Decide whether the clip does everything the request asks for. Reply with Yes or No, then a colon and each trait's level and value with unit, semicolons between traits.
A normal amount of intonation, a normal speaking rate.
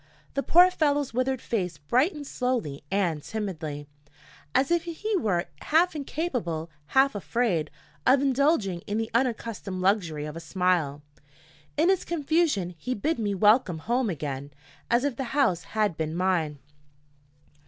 No: wide, 8.2 semitones; average, 145 wpm